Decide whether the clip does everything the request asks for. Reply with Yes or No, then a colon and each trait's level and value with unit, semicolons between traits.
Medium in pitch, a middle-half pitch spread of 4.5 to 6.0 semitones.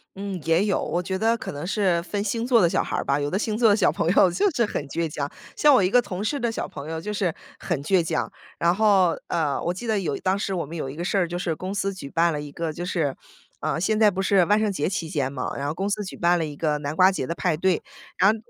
No: medium, 180 Hz; average, 3.9 semitones